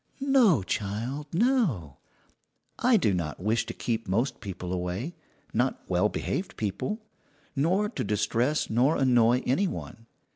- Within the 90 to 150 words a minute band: Yes, slow, 135 wpm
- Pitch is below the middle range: Yes, low, 120 Hz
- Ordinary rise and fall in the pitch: No, wide, 8.0 semitones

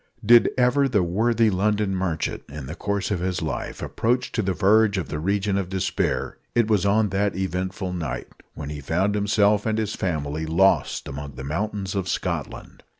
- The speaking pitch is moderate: No, very low, 95 Hz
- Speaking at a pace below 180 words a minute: No, average, 185 wpm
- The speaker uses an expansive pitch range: No, average, 3.6 semitones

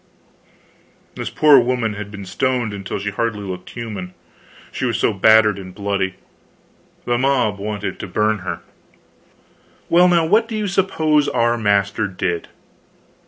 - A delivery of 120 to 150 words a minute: Yes, average, 145 wpm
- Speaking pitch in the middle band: No, low, 110 Hz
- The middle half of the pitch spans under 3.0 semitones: No, average, 4.5 semitones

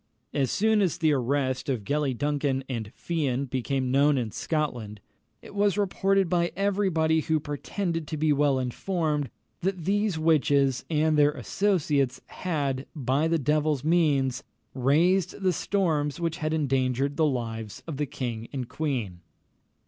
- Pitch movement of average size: Yes, average, 3.9 semitones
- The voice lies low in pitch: No, medium, 150 Hz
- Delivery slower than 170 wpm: Yes, average, 150 wpm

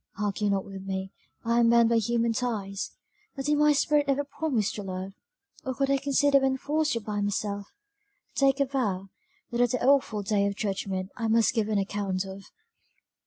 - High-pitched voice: Yes, high, 225 Hz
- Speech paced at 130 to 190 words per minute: No, average, 200 wpm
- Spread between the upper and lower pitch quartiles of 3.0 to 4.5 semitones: No, average, 5.1 semitones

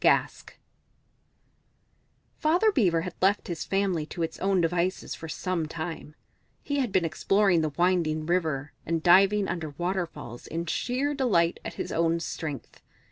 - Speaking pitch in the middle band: Yes, medium, 175 Hz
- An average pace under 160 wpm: Yes, average, 145 wpm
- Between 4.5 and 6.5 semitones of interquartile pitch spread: No, average, 3.2 semitones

